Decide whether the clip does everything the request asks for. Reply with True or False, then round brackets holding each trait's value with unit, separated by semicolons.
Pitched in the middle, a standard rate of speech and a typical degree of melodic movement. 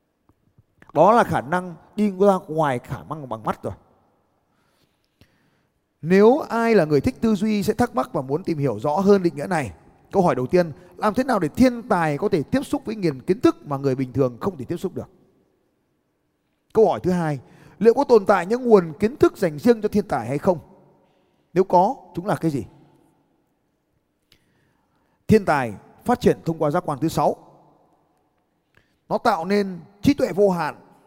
False (180 Hz; 195 wpm; 5.7 semitones)